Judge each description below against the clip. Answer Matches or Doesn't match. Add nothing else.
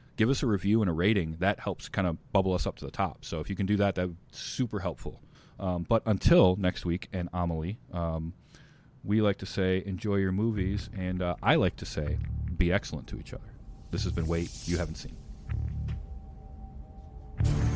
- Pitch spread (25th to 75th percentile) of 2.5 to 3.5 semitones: Matches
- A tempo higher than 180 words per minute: Matches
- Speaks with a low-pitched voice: Matches